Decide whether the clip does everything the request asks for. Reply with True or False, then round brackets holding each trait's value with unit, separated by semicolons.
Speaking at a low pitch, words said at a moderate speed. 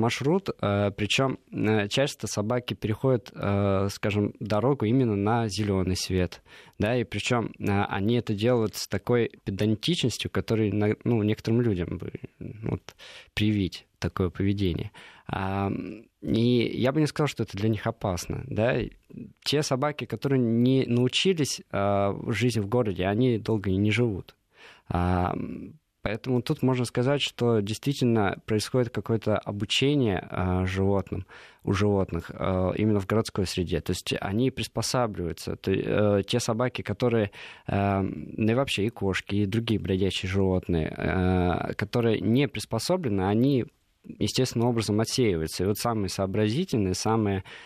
True (110 Hz; 130 wpm)